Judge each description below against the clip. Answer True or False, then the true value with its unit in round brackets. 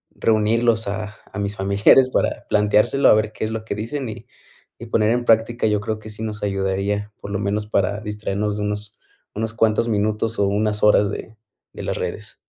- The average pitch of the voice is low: True (105 Hz)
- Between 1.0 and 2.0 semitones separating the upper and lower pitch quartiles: True (1.4 semitones)